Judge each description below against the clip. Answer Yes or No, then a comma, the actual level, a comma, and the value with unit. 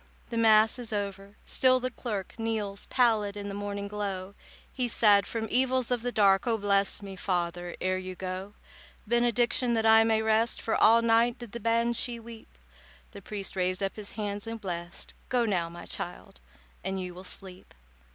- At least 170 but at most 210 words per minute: Yes, average, 180 wpm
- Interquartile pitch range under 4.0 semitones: Yes, average, 3.2 semitones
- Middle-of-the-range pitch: No, high, 210 Hz